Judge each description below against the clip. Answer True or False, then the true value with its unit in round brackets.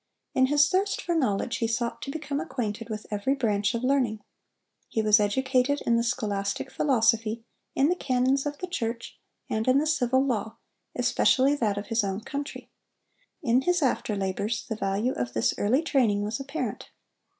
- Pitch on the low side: False (240 Hz)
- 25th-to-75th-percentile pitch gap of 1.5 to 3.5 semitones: False (4.4 semitones)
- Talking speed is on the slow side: False (175 wpm)